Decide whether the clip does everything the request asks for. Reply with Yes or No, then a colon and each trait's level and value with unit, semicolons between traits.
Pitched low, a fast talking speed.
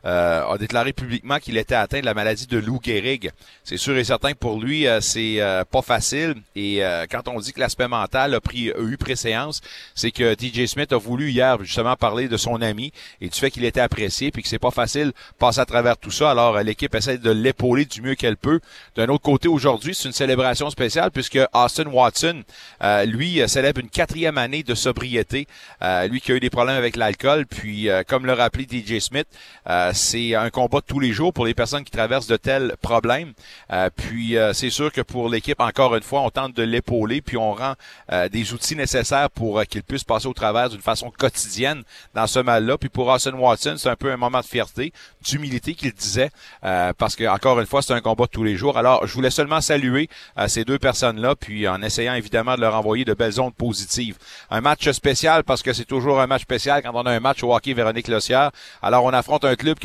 Yes: low, 125 Hz; fast, 235 wpm